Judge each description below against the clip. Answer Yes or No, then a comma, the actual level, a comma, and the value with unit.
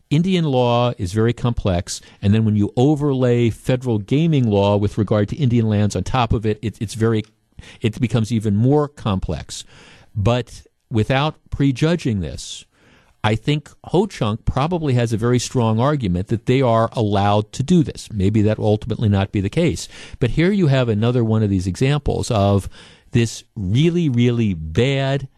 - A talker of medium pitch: No, low, 115 Hz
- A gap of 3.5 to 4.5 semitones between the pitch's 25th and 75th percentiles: Yes, average, 4.0 semitones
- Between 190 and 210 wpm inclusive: No, average, 175 wpm